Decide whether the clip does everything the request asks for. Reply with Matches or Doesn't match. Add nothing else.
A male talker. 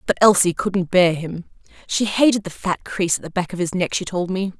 Doesn't match